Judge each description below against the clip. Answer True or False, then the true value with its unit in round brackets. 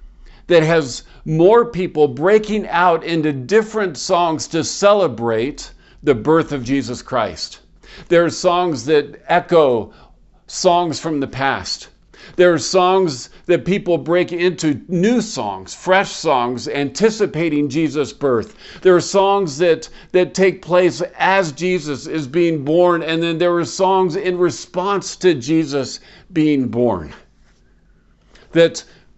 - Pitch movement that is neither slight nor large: True (3.5 semitones)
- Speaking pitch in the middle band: True (170 Hz)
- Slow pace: True (130 wpm)